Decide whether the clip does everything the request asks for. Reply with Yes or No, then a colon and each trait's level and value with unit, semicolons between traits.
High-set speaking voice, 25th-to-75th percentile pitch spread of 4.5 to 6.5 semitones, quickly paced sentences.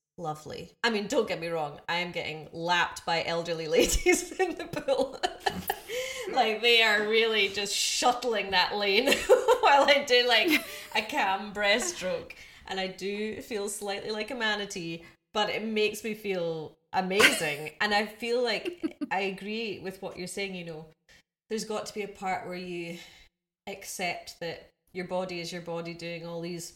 No: high, 200 Hz; average, 5.0 semitones; average, 170 wpm